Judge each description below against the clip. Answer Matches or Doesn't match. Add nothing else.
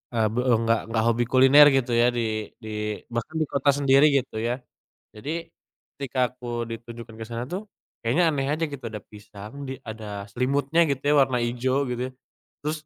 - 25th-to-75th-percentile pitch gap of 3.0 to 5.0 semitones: Matches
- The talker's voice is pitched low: Matches